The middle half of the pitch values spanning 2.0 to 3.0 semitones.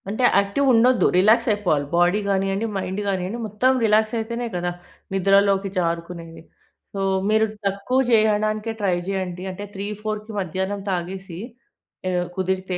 Yes: narrow, 2.6 semitones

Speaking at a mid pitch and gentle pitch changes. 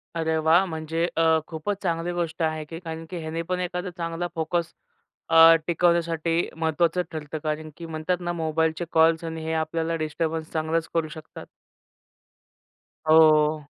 Yes: medium, 160 Hz; narrow, 1.1 semitones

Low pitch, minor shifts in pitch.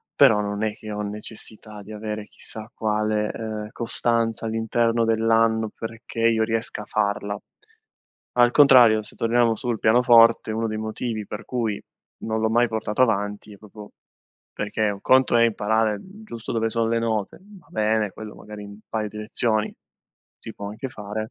Yes: low, 110 Hz; narrow, 1.4 semitones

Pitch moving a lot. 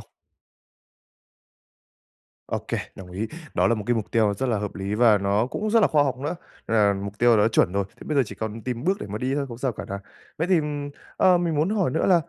Yes: wide, 6.1 semitones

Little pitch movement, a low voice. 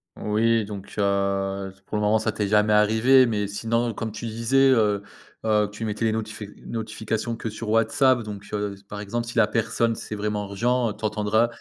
Yes: narrow, 1.8 semitones; low, 110 Hz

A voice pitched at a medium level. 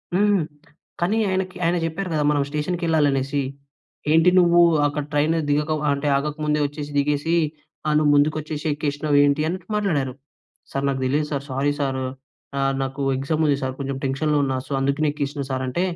Yes: medium, 150 Hz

